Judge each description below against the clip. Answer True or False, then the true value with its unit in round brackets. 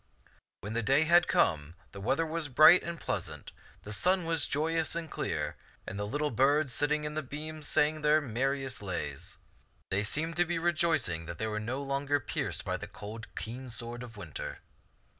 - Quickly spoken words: False (185 wpm)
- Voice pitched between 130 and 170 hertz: True (140 Hz)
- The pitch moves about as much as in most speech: False (6.1 semitones)